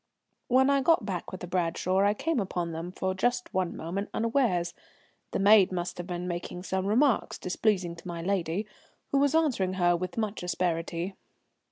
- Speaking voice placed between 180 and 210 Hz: Yes, medium, 185 Hz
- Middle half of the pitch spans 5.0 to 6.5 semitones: No, average, 3.8 semitones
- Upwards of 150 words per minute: Yes, average, 180 wpm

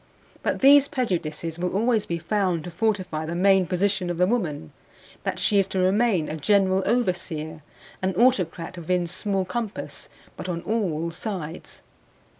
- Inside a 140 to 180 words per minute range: Yes, average, 155 wpm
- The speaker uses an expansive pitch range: No, average, 3.4 semitones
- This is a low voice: No, medium, 185 Hz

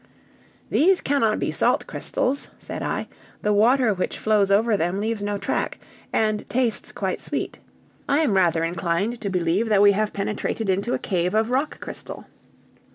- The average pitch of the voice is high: Yes, high, 210 Hz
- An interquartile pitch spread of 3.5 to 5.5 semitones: No, average, 3.1 semitones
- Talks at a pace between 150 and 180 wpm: Yes, average, 165 wpm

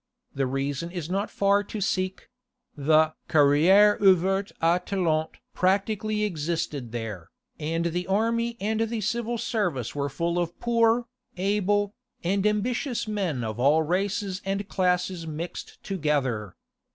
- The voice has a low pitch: No, medium, 185 Hz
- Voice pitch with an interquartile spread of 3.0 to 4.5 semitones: No, average, 4.9 semitones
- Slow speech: Yes, slow, 130 wpm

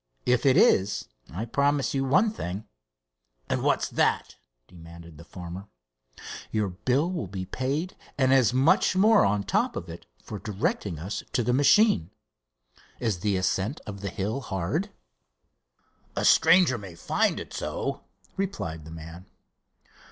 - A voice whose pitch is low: Yes, low, 105 Hz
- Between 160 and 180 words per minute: No, average, 145 wpm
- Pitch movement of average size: No, wide, 7.0 semitones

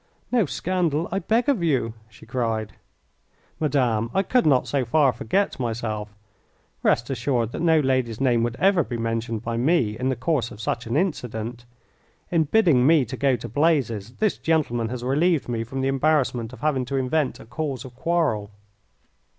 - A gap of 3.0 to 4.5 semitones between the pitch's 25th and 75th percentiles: No, average, 5.2 semitones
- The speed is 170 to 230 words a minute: Yes, average, 180 wpm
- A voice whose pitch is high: No, low, 130 Hz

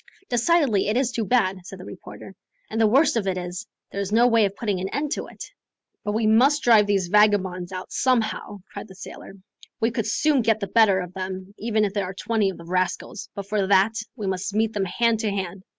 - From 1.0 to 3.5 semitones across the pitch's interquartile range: Yes, average, 3.1 semitones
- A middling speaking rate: No, fast, 230 wpm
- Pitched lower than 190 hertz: No, high, 210 Hz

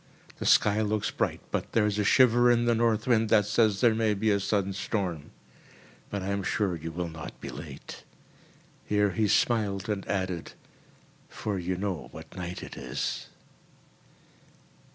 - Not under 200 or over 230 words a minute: No, average, 170 wpm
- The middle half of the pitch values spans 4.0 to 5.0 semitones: No, average, 2.8 semitones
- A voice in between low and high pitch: No, low, 105 Hz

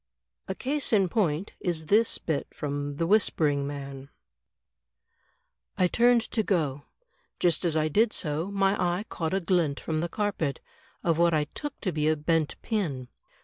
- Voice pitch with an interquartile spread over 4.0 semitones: Yes, average, 5.0 semitones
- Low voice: No, medium, 165 Hz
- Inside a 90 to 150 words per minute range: No, average, 175 wpm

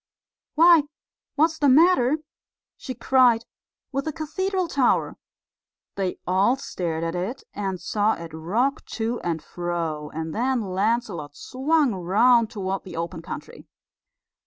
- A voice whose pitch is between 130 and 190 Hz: No, high, 225 Hz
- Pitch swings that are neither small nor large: No, wide, 7.4 semitones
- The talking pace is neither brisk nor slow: No, slow, 130 wpm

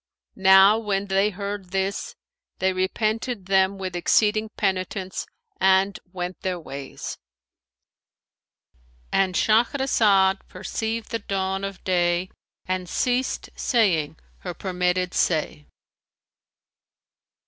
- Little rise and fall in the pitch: Yes, narrow, 2.3 semitones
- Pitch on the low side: No, high, 190 Hz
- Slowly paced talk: Yes, slow, 95 wpm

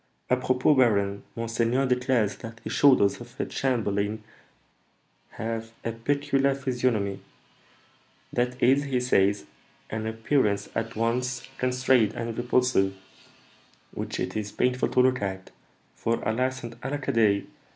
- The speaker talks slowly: Yes, slow, 120 wpm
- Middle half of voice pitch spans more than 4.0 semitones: No, average, 2.8 semitones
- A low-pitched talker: Yes, low, 120 Hz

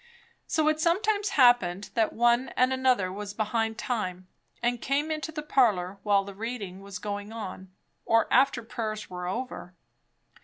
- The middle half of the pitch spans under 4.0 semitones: No, average, 4.6 semitones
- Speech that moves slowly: No, average, 155 wpm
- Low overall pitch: No, high, 225 Hz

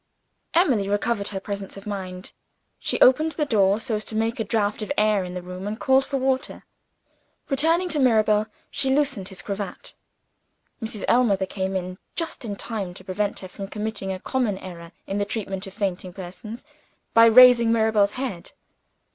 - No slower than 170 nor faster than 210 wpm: Yes, average, 180 wpm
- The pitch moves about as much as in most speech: Yes, average, 3.6 semitones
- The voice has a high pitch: Yes, high, 210 Hz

